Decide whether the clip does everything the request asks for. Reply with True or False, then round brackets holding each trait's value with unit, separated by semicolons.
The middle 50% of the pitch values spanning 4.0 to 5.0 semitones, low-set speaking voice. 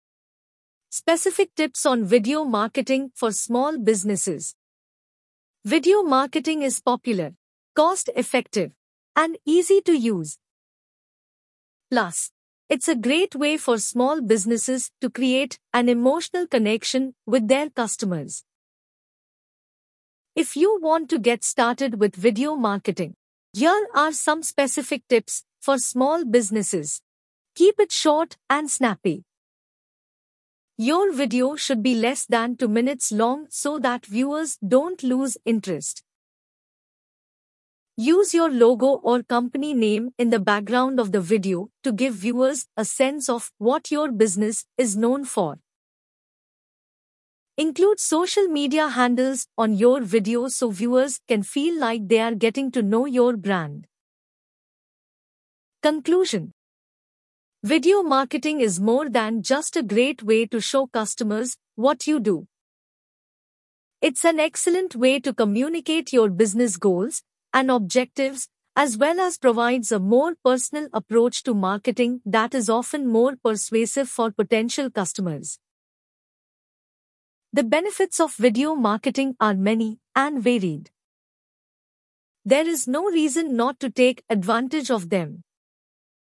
False (4.4 semitones; 250 Hz)